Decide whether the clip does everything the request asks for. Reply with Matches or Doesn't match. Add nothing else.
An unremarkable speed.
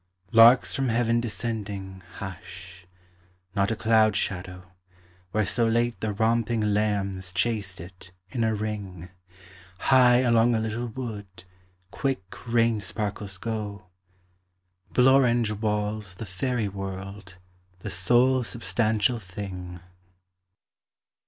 Doesn't match